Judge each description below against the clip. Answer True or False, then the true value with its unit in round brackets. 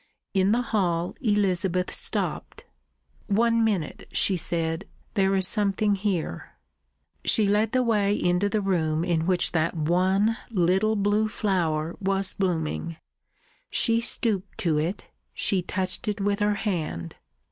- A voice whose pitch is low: False (195 Hz)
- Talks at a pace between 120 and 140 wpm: True (135 wpm)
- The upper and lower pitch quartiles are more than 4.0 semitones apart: False (3.3 semitones)